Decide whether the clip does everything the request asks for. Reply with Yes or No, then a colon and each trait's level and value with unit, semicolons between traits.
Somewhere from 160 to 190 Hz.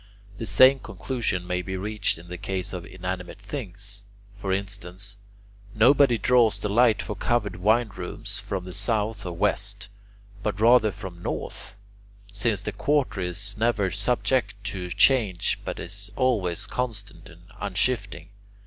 No: low, 100 Hz